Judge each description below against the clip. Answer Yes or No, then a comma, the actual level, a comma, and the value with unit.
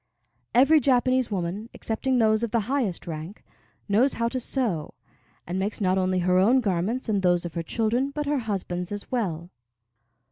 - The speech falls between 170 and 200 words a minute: Yes, average, 175 wpm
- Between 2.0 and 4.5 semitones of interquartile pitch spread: No, wide, 5.4 semitones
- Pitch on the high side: Yes, high, 215 Hz